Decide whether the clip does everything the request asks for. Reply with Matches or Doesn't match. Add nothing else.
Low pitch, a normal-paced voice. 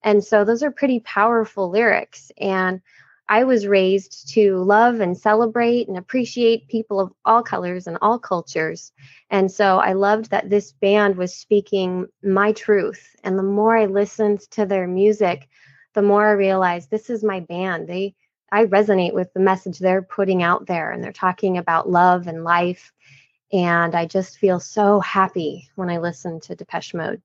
Doesn't match